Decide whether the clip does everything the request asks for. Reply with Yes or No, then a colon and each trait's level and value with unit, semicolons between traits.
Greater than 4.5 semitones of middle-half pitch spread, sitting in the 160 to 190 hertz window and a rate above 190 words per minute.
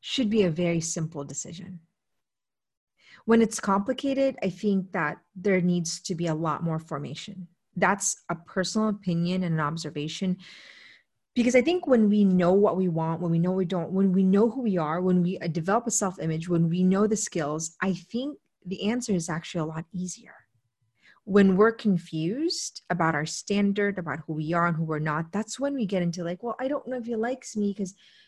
No: average, 3.8 semitones; medium, 185 Hz; average, 200 wpm